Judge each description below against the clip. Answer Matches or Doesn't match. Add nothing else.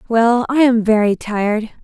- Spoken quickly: Doesn't match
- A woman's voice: Matches